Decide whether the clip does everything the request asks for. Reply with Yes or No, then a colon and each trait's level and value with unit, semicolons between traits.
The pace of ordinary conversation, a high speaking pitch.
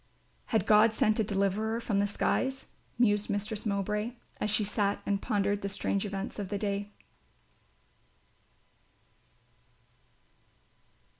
No: slow, 120 wpm; high, 205 Hz